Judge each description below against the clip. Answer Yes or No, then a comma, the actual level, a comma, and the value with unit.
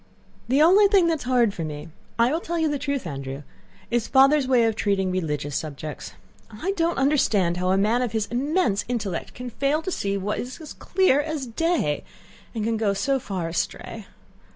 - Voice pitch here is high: Yes, high, 235 Hz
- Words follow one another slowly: No, average, 200 wpm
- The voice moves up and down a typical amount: No, wide, 7.3 semitones